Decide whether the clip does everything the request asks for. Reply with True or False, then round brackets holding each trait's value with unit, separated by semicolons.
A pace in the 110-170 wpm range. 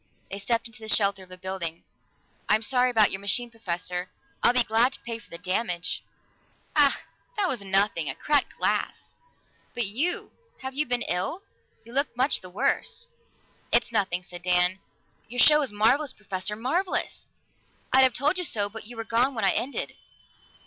False (180 wpm)